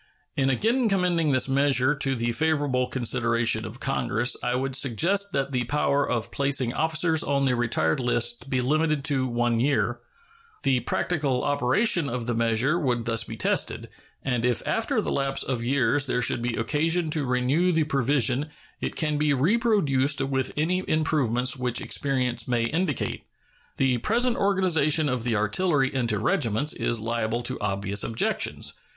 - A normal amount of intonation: Yes, average, 4.0 semitones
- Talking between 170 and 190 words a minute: No, average, 160 wpm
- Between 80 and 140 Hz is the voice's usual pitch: Yes, low, 135 Hz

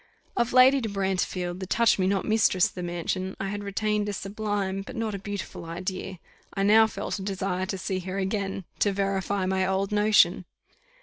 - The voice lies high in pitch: Yes, high, 195 Hz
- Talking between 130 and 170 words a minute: No, average, 200 wpm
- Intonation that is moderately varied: No, narrow, 1.8 semitones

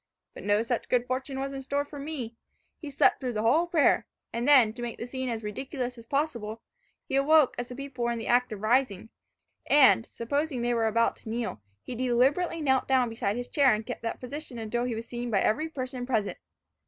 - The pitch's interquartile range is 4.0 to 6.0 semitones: No, average, 3.0 semitones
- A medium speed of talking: No, fast, 225 wpm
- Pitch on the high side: Yes, high, 245 Hz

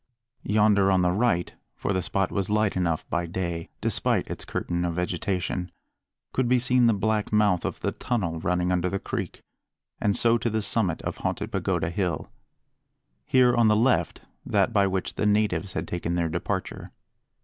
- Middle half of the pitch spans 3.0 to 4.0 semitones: Yes, average, 3.4 semitones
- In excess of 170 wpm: Yes, average, 180 wpm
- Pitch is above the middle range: No, very low, 95 Hz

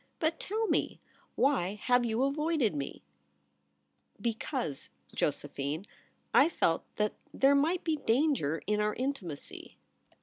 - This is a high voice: Yes, high, 220 Hz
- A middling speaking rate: No, slow, 130 wpm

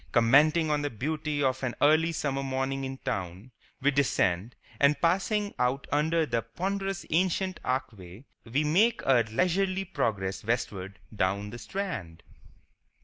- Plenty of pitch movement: Yes, wide, 6.2 semitones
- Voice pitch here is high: No, low, 135 Hz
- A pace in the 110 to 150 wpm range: Yes, average, 140 wpm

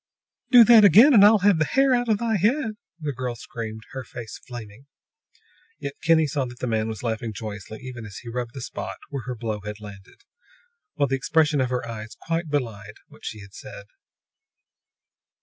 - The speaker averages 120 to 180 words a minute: No, average, 195 wpm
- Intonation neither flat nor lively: No, wide, 6.9 semitones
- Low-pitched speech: Yes, low, 125 Hz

